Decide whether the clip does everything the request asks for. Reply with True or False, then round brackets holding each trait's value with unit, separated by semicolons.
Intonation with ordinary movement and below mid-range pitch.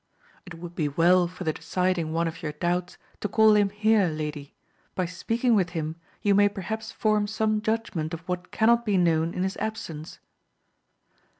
False (4.3 semitones; 180 Hz)